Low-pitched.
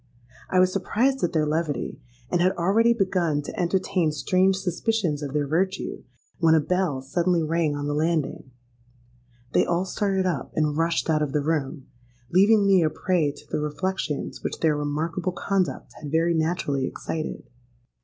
No: medium, 165 Hz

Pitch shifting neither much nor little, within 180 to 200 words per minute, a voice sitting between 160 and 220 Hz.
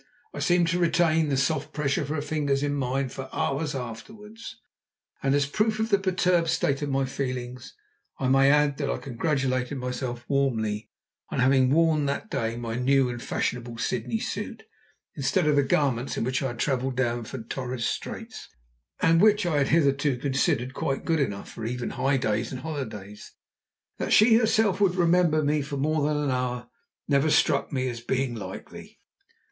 No: average, 3.7 semitones; average, 185 wpm; low, 135 Hz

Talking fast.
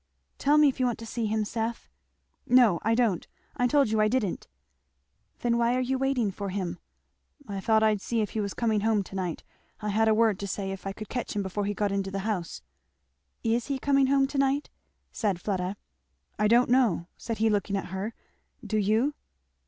Yes: fast, 215 wpm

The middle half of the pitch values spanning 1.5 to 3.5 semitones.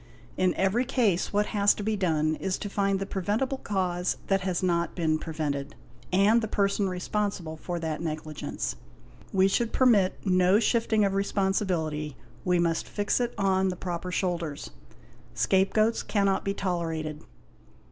Yes: average, 3.1 semitones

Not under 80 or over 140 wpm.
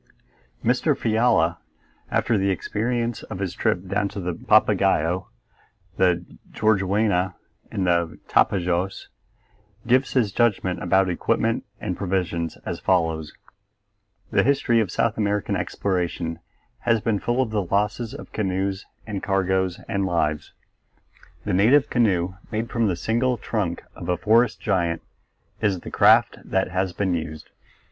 Yes: slow, 135 wpm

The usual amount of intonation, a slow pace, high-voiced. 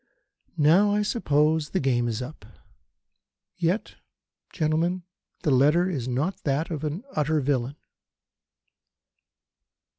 No: average, 4.1 semitones; slow, 110 wpm; medium, 155 Hz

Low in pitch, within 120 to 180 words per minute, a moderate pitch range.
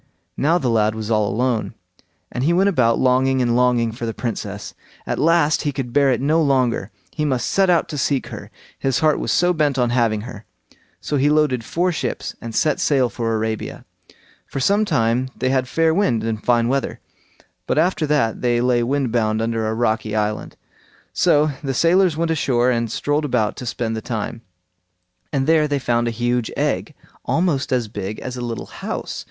No: low, 125 Hz; average, 195 wpm; average, 4.4 semitones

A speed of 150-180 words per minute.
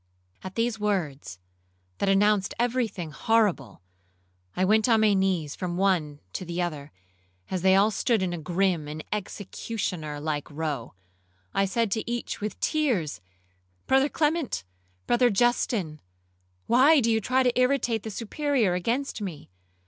No: average, 140 wpm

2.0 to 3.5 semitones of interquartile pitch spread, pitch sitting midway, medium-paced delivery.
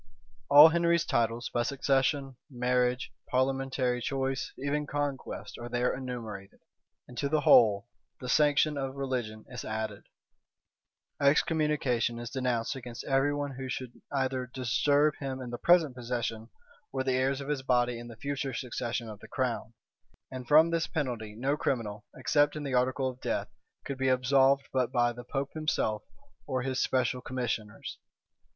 No: narrow, 2.5 semitones; low, 130 Hz; average, 160 wpm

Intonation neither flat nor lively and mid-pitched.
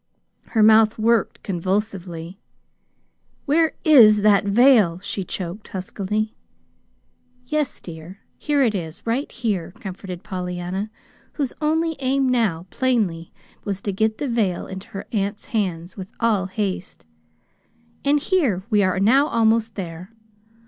No: average, 4.0 semitones; high, 210 Hz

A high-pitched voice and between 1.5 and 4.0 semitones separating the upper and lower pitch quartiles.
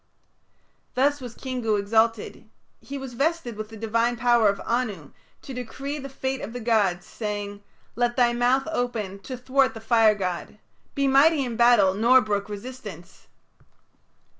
Yes: high, 235 Hz; average, 3.6 semitones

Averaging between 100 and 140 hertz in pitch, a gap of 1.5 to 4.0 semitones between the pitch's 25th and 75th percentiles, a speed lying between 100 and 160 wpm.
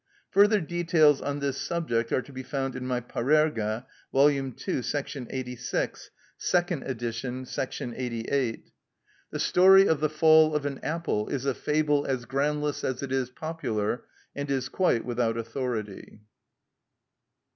Yes: low, 135 Hz; average, 3.6 semitones; average, 145 wpm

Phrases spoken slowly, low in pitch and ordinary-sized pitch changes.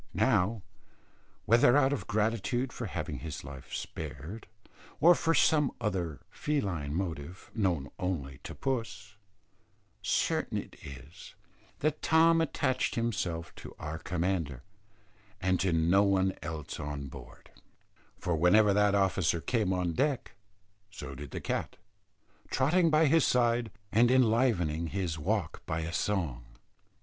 No: slow, 130 wpm; very low, 95 Hz; wide, 6.8 semitones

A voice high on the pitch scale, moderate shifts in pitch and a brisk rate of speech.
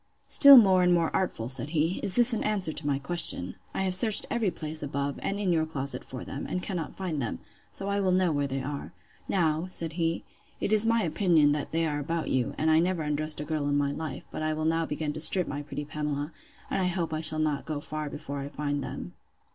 No: medium, 155 Hz; average, 3.8 semitones; fast, 235 wpm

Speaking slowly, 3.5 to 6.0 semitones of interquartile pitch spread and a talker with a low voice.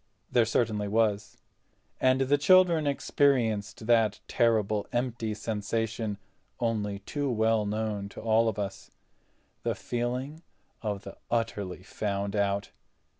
No: slow, 115 wpm; average, 2.8 semitones; low, 110 Hz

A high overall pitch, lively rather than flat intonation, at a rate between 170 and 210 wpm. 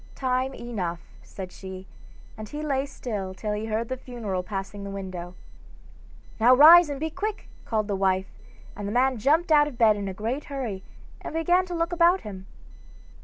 Yes: high, 230 Hz; wide, 6.7 semitones; average, 185 wpm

